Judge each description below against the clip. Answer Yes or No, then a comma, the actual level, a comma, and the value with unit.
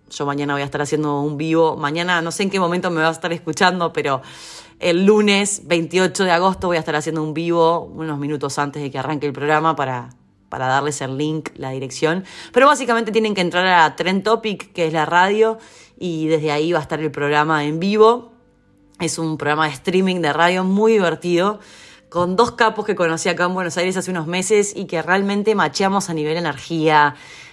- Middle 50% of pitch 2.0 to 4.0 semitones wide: Yes, average, 3.5 semitones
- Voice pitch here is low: No, medium, 170 Hz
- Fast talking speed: Yes, fast, 210 wpm